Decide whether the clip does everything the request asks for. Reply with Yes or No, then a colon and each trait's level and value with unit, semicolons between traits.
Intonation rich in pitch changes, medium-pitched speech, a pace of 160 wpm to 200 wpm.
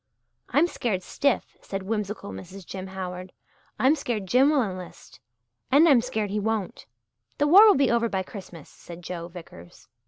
No: wide, 5.8 semitones; high, 205 Hz; average, 165 wpm